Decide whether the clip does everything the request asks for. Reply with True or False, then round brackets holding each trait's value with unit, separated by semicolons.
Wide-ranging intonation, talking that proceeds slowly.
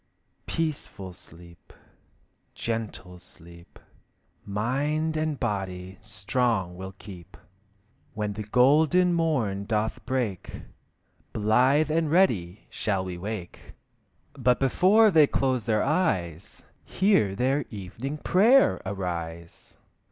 True (7.8 semitones; 100 wpm)